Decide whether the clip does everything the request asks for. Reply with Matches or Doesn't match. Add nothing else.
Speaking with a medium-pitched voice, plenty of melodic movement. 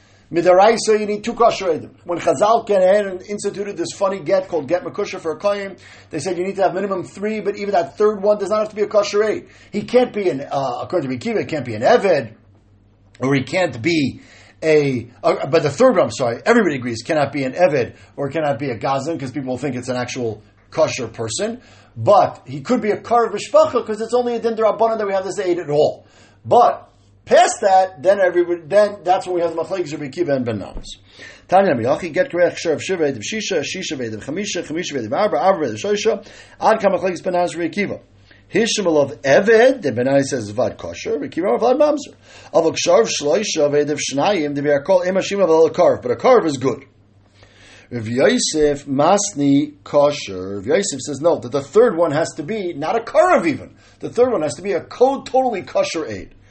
Matches